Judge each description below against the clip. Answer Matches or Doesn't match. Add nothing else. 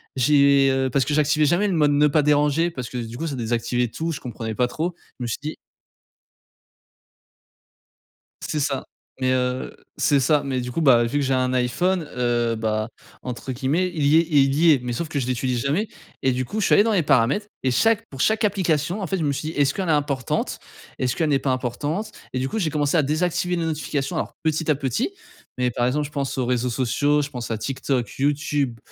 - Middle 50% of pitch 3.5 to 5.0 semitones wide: Matches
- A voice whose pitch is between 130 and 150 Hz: Matches